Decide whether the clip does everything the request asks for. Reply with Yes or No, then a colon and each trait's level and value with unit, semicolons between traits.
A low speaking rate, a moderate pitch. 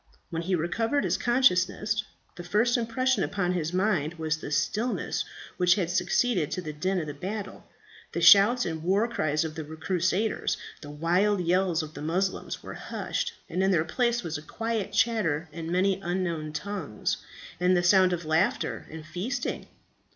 No: average, 170 wpm; medium, 180 Hz